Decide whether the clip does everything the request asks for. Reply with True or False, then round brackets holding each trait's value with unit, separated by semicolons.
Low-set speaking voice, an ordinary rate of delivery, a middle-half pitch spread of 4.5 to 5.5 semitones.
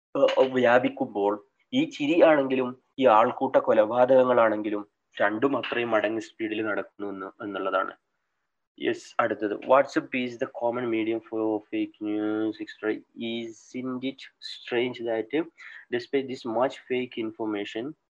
False (125 Hz; 95 wpm; 4.0 semitones)